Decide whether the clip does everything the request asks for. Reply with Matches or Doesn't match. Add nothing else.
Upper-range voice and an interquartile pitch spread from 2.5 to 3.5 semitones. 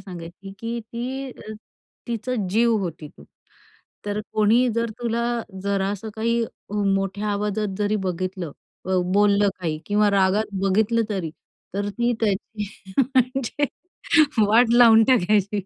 Matches